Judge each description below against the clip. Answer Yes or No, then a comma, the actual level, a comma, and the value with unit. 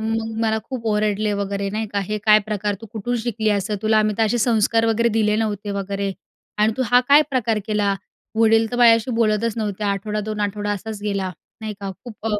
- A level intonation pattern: Yes, narrow, 1.5 semitones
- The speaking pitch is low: No, high, 215 Hz